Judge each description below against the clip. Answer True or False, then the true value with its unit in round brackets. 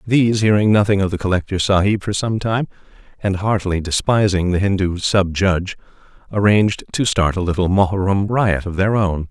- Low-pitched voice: True (95 Hz)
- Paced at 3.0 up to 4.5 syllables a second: False (5.5 syllables/s)